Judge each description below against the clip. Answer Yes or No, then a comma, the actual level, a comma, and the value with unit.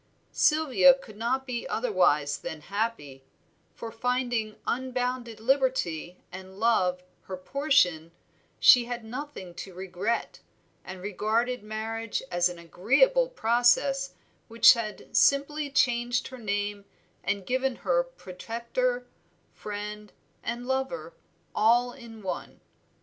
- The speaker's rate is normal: No, slow, 110 wpm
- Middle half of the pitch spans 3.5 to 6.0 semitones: Yes, average, 4.5 semitones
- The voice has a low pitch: No, high, 230 Hz